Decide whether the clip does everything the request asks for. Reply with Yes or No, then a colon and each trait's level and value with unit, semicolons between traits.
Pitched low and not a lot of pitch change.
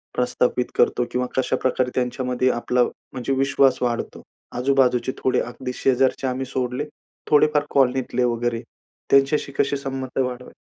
Yes: low, 130 Hz; narrow, 1.4 semitones